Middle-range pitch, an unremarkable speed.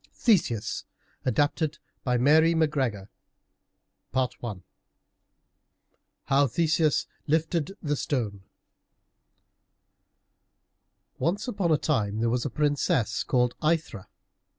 No: medium, 145 Hz; slow, 85 wpm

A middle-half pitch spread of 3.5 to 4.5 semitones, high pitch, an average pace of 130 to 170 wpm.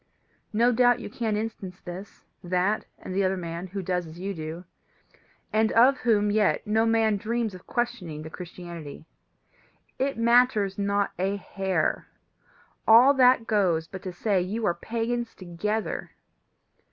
Yes: average, 3.9 semitones; high, 205 Hz; average, 150 wpm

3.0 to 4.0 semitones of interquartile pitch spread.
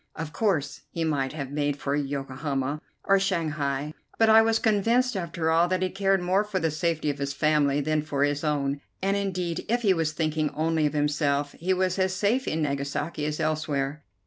No: average, 4.4 semitones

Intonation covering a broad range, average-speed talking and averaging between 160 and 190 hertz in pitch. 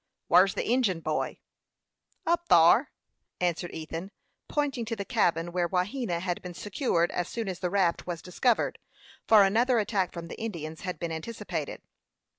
No: average, 4.9 semitones; average, 160 wpm; medium, 185 Hz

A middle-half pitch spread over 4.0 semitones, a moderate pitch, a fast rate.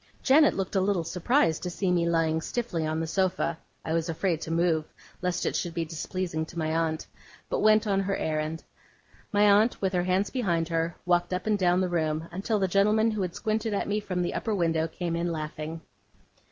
No: average, 3.3 semitones; medium, 175 Hz; fast, 215 wpm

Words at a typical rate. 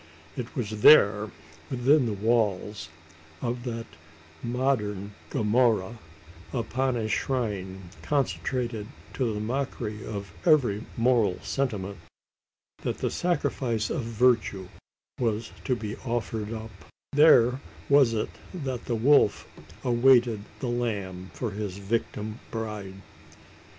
No: slow, 110 wpm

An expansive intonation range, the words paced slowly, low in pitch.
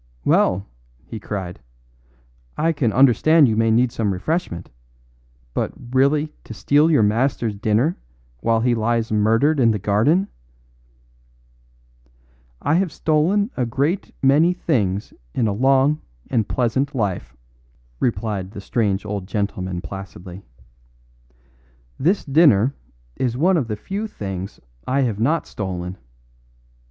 Yes: wide, 6.3 semitones; slow, 125 wpm; low, 115 Hz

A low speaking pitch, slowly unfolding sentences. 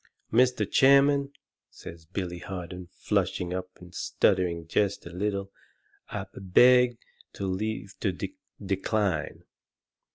Yes: very low, 95 Hz; slow, 120 wpm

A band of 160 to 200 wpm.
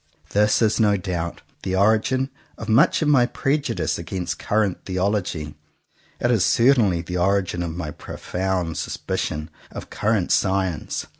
No: average, 145 wpm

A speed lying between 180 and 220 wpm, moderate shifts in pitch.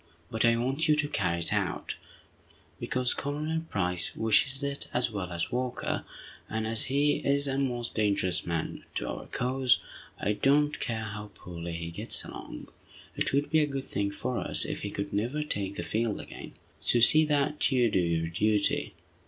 No: average, 185 wpm; wide, 5.7 semitones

